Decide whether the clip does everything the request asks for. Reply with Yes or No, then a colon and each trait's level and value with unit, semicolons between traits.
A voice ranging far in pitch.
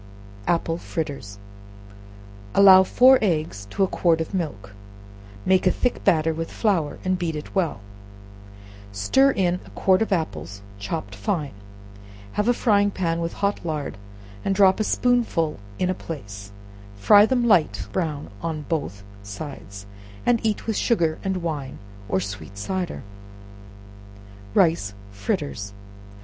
Yes: wide, 6.4 semitones